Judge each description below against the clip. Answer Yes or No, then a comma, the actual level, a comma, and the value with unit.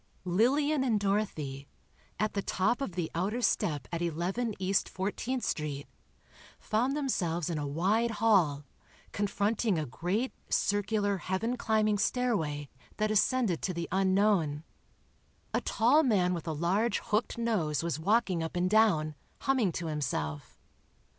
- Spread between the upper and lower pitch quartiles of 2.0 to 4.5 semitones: No, average, 5.1 semitones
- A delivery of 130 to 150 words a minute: Yes, average, 140 wpm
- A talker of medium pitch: No, high, 195 Hz